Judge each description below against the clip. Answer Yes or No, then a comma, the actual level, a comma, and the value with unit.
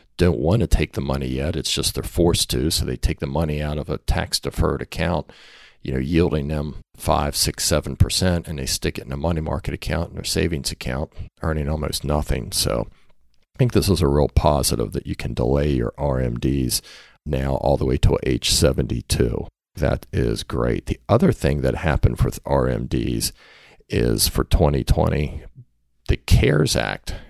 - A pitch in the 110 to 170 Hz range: No, very low, 75 Hz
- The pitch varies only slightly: No, average, 3.5 semitones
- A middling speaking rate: Yes, average, 185 wpm